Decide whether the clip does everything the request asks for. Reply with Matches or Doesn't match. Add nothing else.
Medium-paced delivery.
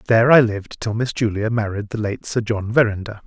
Doesn't match